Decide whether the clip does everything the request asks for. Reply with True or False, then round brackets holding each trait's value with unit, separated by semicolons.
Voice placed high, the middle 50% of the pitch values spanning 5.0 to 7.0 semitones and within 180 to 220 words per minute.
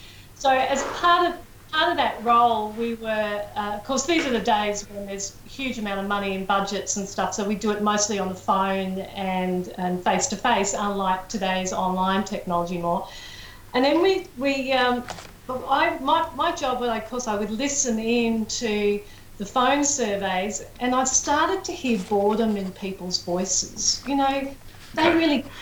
True (215 Hz; 5.3 semitones; 185 wpm)